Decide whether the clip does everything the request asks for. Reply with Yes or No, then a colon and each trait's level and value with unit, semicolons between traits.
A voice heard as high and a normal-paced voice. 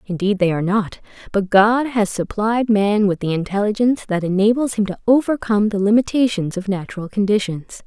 Yes: high, 205 Hz; average, 170 wpm